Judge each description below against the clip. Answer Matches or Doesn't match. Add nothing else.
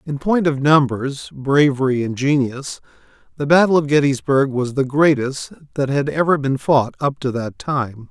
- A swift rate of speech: Doesn't match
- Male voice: Matches